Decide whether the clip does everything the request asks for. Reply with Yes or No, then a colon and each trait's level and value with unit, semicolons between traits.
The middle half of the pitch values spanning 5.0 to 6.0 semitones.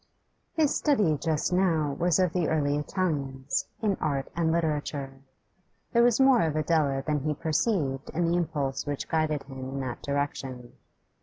No: average, 3.7 semitones